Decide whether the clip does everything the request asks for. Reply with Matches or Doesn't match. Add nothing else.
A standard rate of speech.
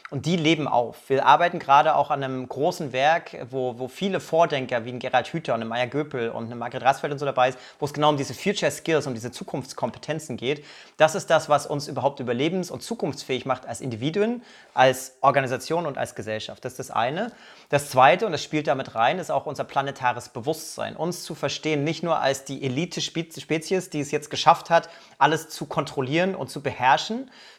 Doesn't match